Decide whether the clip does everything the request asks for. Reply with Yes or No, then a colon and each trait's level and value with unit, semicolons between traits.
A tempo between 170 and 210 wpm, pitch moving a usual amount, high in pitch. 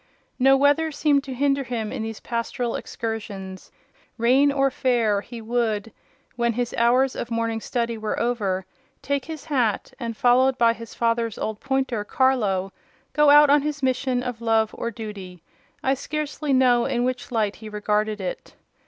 No: average, 160 wpm; average, 3.3 semitones; high, 240 Hz